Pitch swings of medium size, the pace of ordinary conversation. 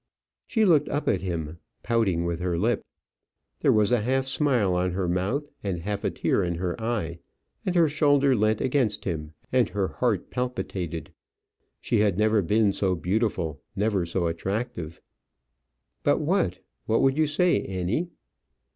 No: wide, 6.0 semitones; average, 160 wpm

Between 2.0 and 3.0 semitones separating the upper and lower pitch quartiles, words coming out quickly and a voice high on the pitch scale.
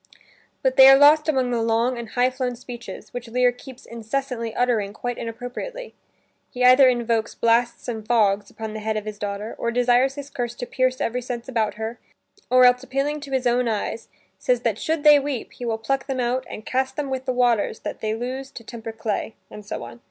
Yes: narrow, 2.5 semitones; fast, 210 wpm; high, 245 Hz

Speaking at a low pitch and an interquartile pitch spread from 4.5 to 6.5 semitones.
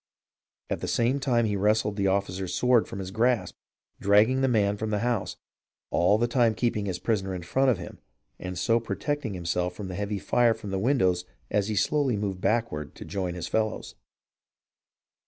No: low, 105 Hz; average, 3.7 semitones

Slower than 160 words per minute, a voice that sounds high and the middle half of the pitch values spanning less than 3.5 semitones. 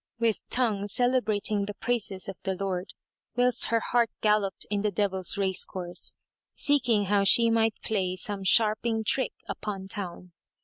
Yes: average, 150 wpm; high, 205 Hz; average, 2.9 semitones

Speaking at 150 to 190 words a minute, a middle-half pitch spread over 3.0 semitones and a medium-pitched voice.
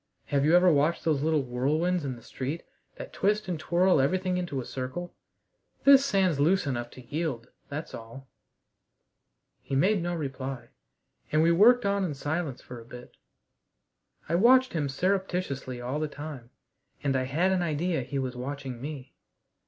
Yes: average, 170 wpm; average, 5.2 semitones; medium, 150 Hz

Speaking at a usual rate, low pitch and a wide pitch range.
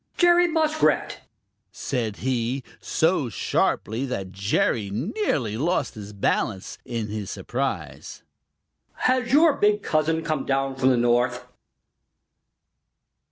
No: slow, 110 wpm; low, 130 Hz; wide, 8.6 semitones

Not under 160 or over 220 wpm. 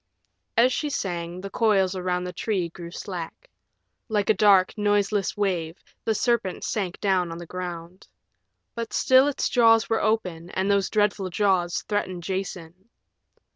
No: average, 150 wpm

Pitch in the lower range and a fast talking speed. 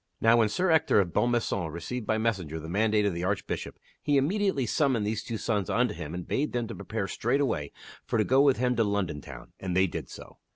Yes: low, 110 Hz; fast, 225 wpm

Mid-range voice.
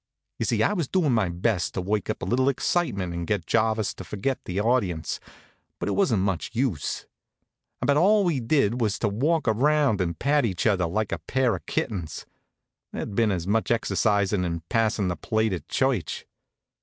No: low, 110 Hz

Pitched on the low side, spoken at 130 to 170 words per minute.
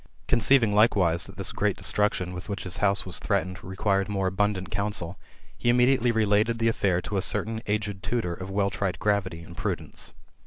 No: low, 100 Hz; average, 185 wpm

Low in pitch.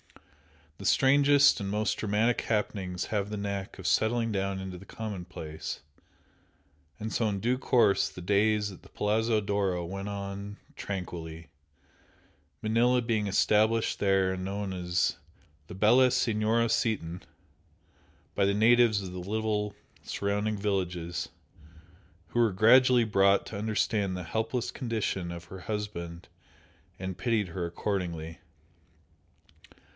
Yes: low, 100 Hz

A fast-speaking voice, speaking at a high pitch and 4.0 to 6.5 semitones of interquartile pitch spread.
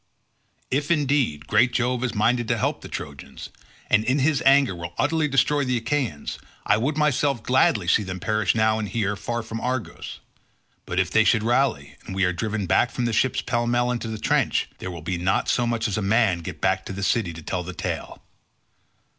No: fast, 215 wpm; low, 115 Hz; average, 4.8 semitones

